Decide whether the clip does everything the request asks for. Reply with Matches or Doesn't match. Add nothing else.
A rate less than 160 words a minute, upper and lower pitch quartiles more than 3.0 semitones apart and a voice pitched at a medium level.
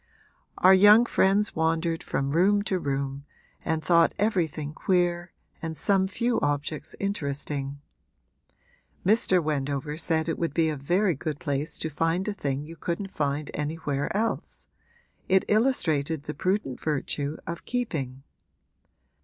Matches